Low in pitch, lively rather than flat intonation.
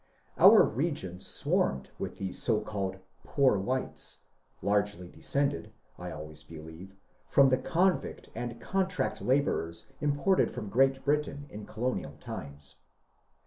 Yes: low, 110 Hz; wide, 7.3 semitones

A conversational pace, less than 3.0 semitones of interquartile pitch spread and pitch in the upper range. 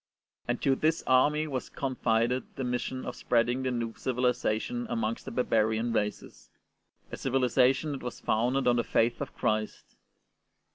No: average, 150 wpm; narrow, 2.4 semitones; low, 125 Hz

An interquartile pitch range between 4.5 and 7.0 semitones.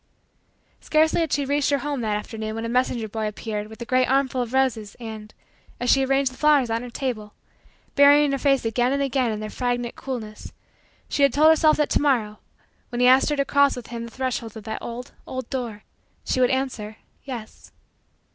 No: average, 3.7 semitones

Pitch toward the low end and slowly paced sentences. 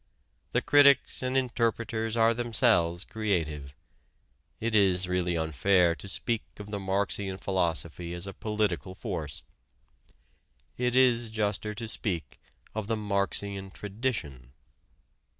Yes: low, 100 Hz; slow, 115 wpm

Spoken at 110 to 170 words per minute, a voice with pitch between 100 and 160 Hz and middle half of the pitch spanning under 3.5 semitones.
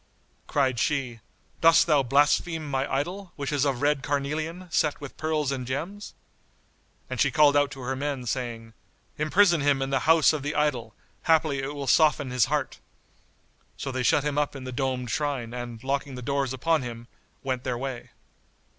No: average, 180 wpm; medium, 140 Hz; average, 2.7 semitones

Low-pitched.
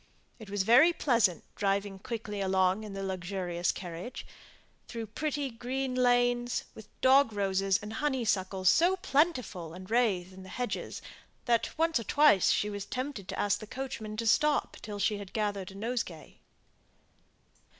No: high, 215 Hz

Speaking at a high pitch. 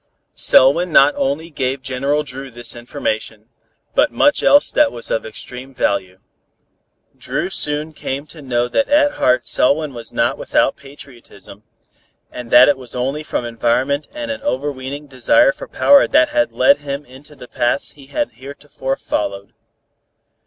No: low, 135 Hz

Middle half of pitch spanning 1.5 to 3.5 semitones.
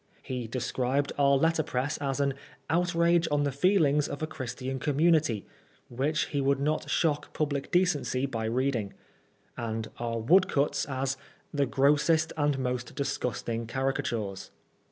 Yes: average, 3.1 semitones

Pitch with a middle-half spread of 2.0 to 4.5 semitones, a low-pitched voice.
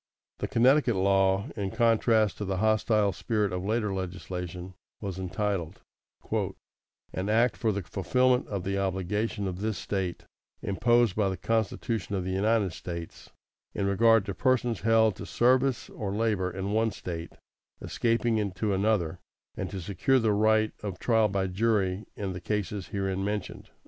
Yes: average, 2.8 semitones; low, 100 Hz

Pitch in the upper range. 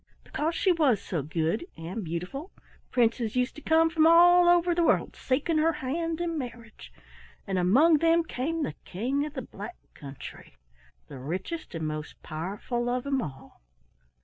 Yes: very high, 260 Hz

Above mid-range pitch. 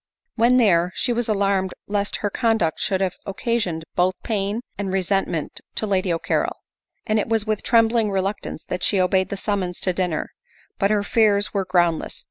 Yes: high, 200 Hz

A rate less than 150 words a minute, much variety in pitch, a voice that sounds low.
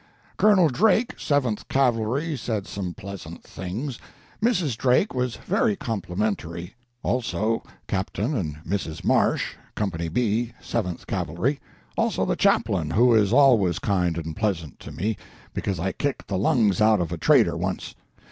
Yes: average, 140 wpm; wide, 5.9 semitones; low, 110 Hz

